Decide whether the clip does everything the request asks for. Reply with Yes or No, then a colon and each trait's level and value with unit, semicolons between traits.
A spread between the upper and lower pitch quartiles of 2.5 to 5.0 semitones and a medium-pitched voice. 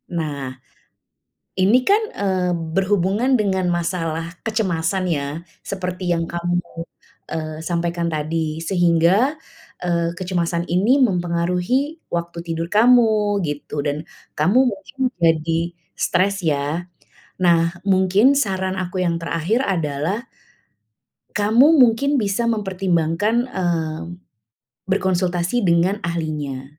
Yes: average, 2.9 semitones; medium, 175 Hz